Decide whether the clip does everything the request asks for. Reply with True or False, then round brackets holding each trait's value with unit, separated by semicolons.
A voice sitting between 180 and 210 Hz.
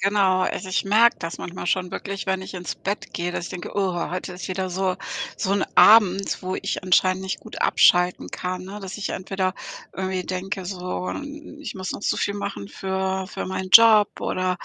True (190 Hz)